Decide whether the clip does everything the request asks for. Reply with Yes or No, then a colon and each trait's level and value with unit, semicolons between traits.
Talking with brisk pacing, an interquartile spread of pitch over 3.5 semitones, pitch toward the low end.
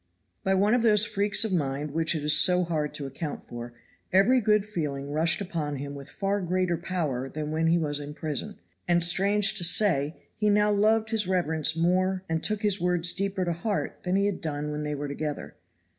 No: fast, 210 wpm; average, 4.9 semitones; medium, 175 Hz